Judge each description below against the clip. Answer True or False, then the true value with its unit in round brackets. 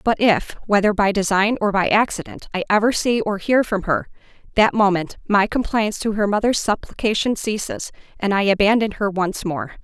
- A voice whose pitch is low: False (205 Hz)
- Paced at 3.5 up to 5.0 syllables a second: False (5.2 syllables/s)